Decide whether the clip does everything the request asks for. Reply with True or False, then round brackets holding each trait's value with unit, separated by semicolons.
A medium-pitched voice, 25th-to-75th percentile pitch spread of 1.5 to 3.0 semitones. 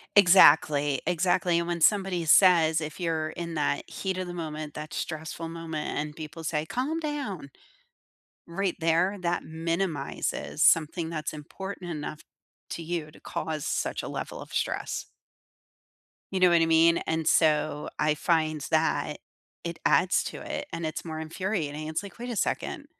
True (165 Hz; 2.4 semitones)